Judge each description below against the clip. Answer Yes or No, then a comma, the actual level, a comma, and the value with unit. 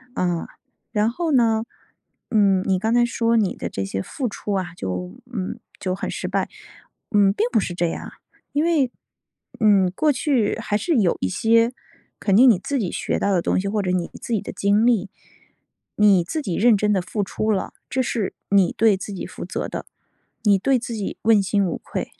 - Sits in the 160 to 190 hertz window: No, high, 205 Hz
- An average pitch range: Yes, average, 3.6 semitones